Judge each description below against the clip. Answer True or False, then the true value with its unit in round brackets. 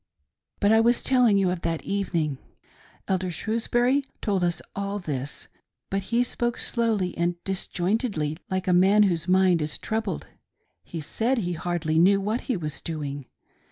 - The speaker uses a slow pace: False (160 wpm)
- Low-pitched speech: False (190 Hz)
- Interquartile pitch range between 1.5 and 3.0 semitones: False (4.5 semitones)